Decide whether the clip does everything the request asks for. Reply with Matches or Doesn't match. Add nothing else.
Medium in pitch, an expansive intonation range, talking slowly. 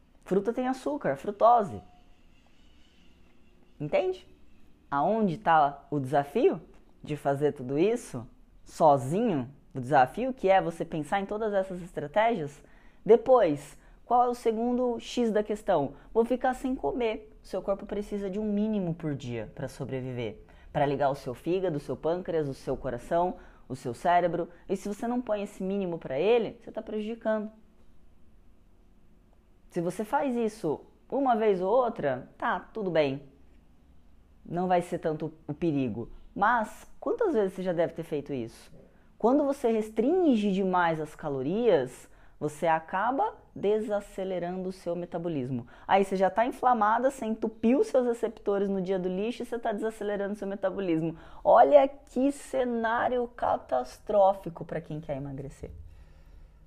Doesn't match